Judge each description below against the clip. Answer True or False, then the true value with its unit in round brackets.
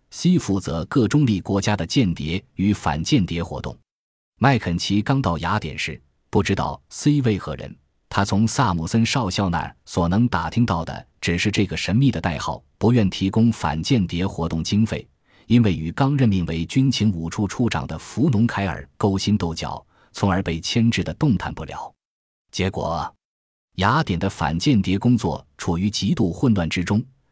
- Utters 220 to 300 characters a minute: True (255 characters per minute)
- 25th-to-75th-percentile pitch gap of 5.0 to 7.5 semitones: True (5.3 semitones)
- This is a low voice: True (100 Hz)